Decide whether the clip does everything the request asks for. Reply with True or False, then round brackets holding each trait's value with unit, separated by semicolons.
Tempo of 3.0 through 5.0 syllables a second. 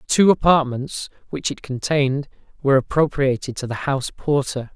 False (5.2 syllables/s)